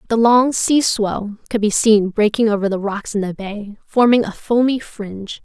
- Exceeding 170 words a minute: Yes, average, 200 wpm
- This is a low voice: No, high, 215 Hz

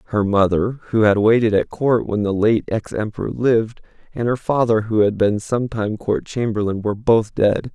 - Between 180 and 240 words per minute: Yes, average, 200 wpm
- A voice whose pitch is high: No, low, 110 Hz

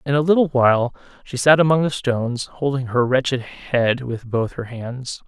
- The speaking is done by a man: Yes, male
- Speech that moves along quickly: No, average, 195 wpm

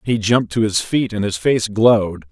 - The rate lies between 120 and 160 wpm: No, fast, 235 wpm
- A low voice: Yes, low, 105 Hz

